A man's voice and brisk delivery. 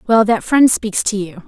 No: female; fast, 245 wpm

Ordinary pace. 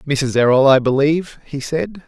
Yes: average, 175 wpm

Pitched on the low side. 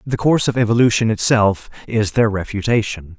Yes: low, 110 Hz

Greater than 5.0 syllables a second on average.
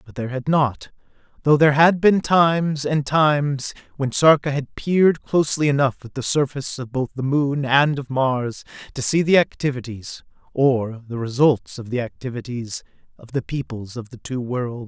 No: 4.9 syllables/s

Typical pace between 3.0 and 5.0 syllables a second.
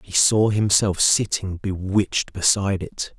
Yes: 4.3 syllables/s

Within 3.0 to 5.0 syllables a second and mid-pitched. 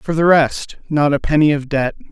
Yes: 4.9 syllables/s; medium, 150 Hz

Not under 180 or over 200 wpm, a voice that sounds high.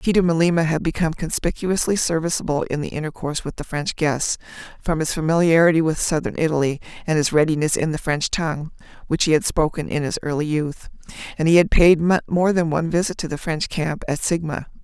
No: average, 195 wpm; medium, 160 Hz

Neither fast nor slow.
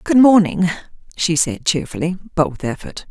Yes: average, 155 wpm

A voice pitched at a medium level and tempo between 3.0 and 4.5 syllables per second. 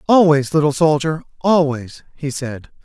Yes: medium, 150 Hz; 4.4 syllables/s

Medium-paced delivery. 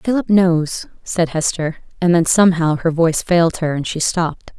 Yes: average, 185 wpm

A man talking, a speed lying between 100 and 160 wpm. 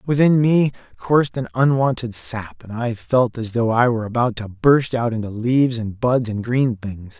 No: male; average, 200 wpm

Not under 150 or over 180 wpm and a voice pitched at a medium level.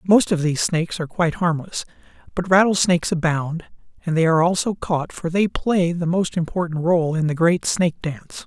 No: average, 190 wpm; medium, 170 Hz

